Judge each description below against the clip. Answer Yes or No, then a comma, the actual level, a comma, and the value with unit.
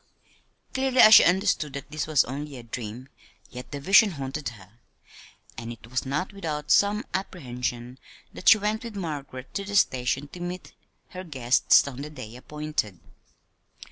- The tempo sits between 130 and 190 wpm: Yes, average, 165 wpm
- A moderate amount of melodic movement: No, wide, 6.8 semitones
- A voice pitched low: No, medium, 145 Hz